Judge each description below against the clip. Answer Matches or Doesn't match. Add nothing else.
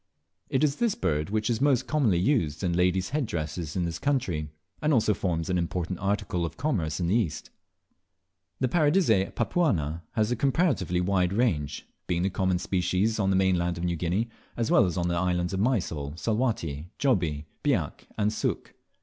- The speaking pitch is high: Doesn't match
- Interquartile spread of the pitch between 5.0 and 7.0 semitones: Matches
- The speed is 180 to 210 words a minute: Matches